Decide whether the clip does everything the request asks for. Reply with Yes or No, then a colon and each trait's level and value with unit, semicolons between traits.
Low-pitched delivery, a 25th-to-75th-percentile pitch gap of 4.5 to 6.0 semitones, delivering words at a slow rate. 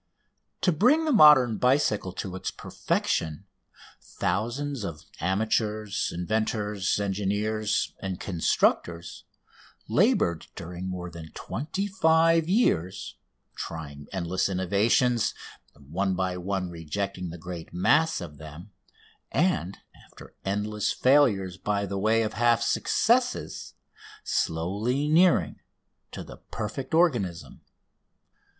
Yes: low, 100 Hz; wide, 5.4 semitones; slow, 105 wpm